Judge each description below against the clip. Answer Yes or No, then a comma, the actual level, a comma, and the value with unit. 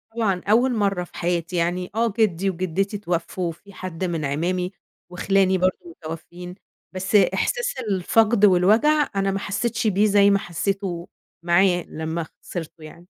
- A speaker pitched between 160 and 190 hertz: Yes, medium, 185 Hz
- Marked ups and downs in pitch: No, narrow, 2.6 semitones